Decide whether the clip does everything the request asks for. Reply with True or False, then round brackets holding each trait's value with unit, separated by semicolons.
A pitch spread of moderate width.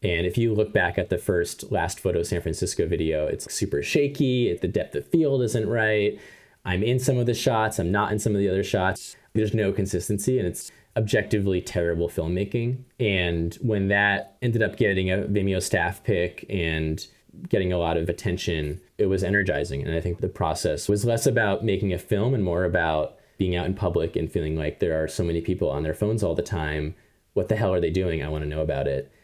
True (4.1 semitones)